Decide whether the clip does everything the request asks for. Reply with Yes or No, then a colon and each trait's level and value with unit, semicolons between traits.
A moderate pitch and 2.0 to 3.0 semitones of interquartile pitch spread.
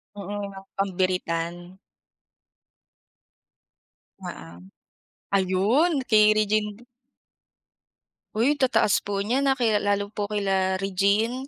No: high, 205 Hz; average, 2.7 semitones